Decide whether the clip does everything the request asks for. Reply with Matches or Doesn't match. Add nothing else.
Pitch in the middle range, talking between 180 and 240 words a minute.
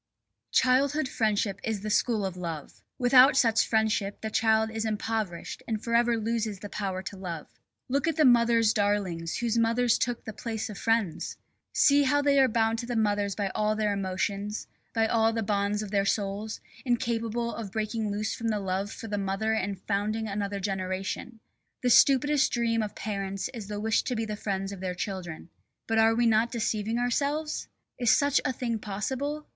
Doesn't match